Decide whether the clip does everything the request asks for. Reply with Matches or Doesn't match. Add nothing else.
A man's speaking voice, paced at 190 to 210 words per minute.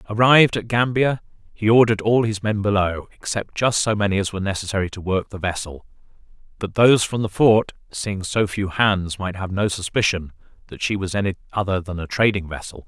Matches